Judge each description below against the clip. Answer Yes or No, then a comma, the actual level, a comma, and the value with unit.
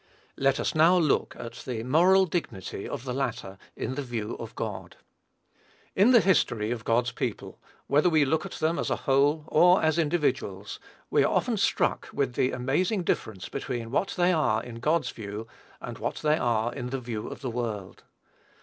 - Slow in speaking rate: No, average, 185 wpm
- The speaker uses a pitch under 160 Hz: Yes, low, 135 Hz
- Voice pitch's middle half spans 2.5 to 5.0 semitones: No, wide, 5.5 semitones